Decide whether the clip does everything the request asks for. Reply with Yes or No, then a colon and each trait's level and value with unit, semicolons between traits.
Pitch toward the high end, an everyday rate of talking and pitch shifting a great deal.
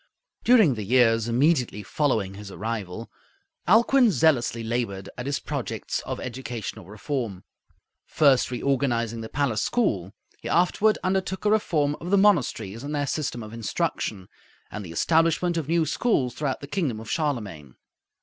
No: low, 125 Hz; average, 150 wpm; wide, 6.4 semitones